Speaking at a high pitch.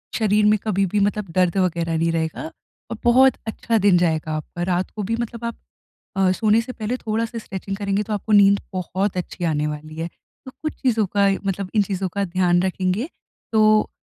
Yes: high, 195 Hz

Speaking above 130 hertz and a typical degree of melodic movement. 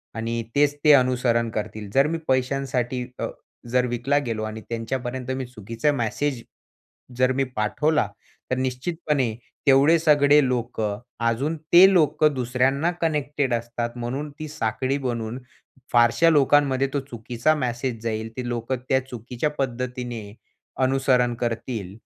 No: low, 125 Hz; average, 3.2 semitones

